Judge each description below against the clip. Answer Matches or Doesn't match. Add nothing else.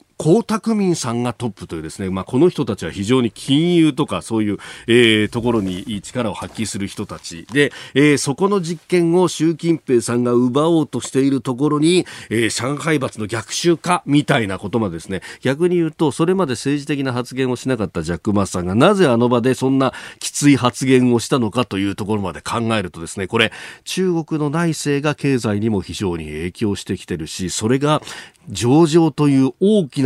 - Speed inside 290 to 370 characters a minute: Doesn't match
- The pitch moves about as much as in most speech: Doesn't match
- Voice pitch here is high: Doesn't match